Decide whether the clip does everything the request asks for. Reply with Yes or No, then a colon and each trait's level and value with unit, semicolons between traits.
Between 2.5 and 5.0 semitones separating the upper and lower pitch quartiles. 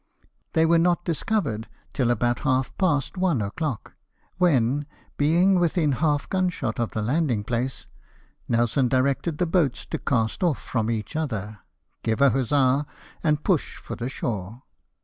No: wide, 5.5 semitones